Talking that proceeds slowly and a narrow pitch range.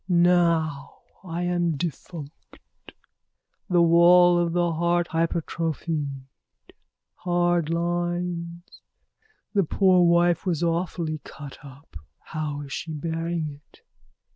Yes: slow, 100 wpm; narrow, 1.8 semitones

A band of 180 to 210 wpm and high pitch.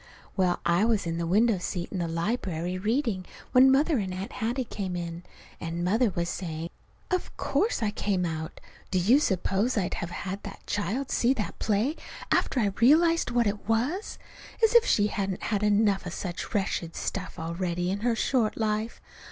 Yes: average, 185 wpm; high, 205 Hz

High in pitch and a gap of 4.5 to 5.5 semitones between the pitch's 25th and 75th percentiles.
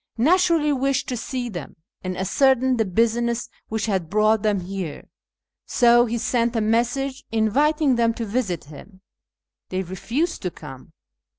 Yes: high, 230 Hz; average, 4.9 semitones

